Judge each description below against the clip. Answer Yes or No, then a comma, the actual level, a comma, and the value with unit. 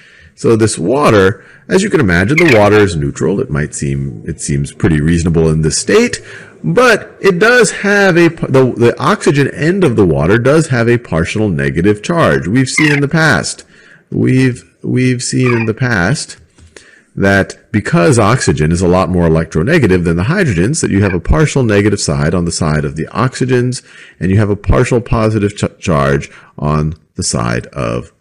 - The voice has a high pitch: No, low, 100 Hz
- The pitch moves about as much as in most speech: No, wide, 7.7 semitones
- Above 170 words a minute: Yes, average, 185 wpm